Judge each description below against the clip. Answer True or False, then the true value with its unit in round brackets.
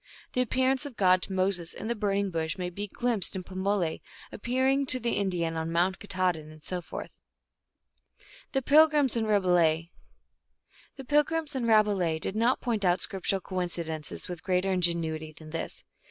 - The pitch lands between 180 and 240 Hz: True (190 Hz)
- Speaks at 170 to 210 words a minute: False (155 wpm)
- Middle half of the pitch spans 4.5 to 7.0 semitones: True (5.3 semitones)